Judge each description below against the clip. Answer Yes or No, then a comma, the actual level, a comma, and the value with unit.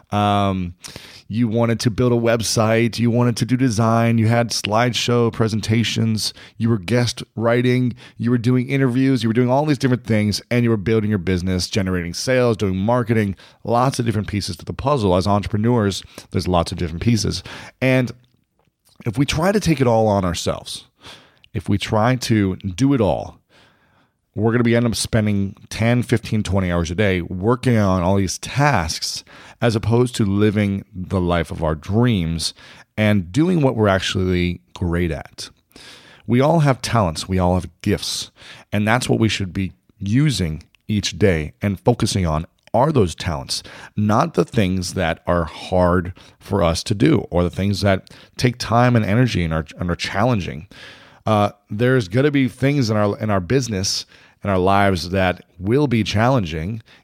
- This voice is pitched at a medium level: No, low, 110 Hz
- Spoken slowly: No, average, 180 wpm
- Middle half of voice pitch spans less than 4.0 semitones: No, average, 4.3 semitones